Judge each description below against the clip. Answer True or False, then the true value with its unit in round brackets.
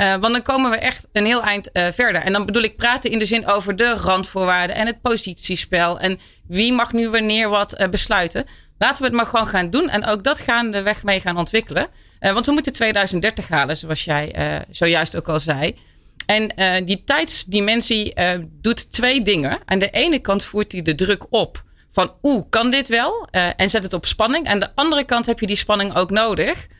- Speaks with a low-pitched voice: False (210 Hz)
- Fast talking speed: True (225 wpm)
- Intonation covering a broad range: False (4.1 semitones)